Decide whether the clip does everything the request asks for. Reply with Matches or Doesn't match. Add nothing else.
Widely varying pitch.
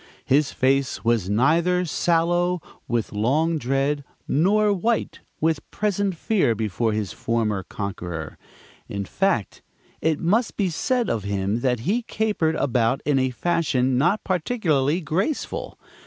Matches